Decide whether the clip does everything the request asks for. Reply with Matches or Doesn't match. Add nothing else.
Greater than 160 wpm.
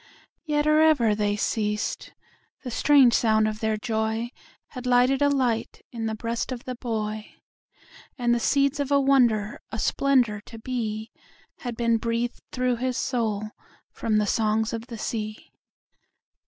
Doesn't match